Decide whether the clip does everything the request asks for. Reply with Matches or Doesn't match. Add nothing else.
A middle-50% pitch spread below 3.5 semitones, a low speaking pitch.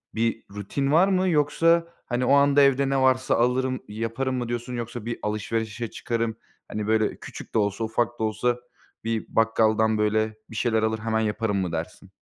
Matches